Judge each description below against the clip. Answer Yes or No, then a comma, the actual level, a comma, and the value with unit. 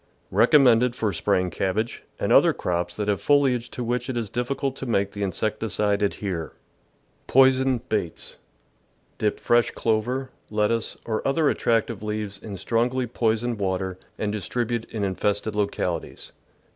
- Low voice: Yes, low, 110 Hz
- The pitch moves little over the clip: No, average, 3.3 semitones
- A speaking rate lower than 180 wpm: Yes, average, 160 wpm